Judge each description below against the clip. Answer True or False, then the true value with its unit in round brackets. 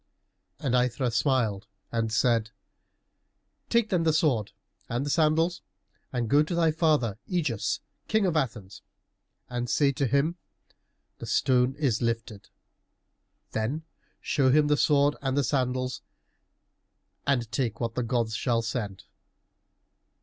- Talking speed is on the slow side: True (130 wpm)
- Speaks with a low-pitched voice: True (130 Hz)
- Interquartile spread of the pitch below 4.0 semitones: False (4.5 semitones)